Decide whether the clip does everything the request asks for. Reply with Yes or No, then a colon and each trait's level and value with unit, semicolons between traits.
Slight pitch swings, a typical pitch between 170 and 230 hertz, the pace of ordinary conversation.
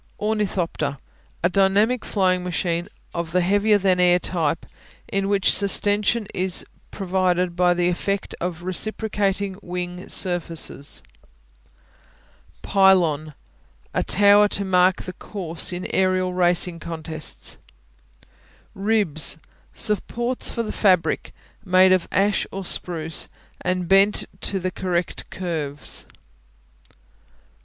No: narrow, 2.2 semitones; medium, 185 Hz; slow, 110 wpm